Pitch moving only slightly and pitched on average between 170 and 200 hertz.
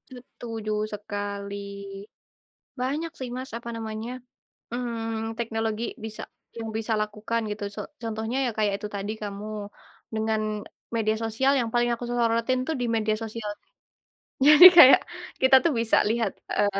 No: narrow, 2.0 semitones; high, 225 Hz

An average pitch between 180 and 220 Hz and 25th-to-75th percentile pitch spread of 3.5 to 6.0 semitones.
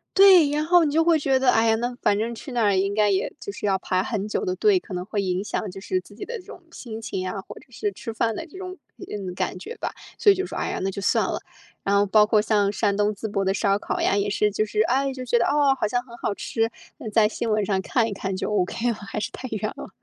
Yes: high, 215 Hz; average, 4.6 semitones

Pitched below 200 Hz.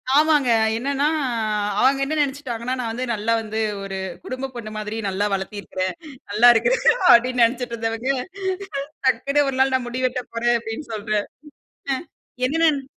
No: high, 245 Hz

